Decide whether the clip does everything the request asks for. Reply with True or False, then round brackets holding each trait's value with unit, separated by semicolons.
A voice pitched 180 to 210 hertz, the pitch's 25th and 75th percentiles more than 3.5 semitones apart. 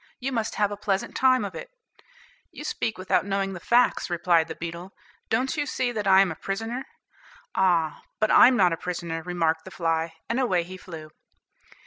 True (190 Hz; 4.8 semitones)